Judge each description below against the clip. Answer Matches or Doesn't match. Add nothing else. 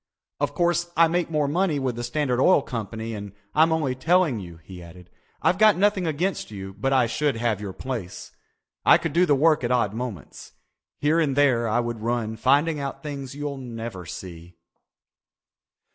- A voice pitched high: Doesn't match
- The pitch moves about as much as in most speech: Doesn't match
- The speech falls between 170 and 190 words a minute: Matches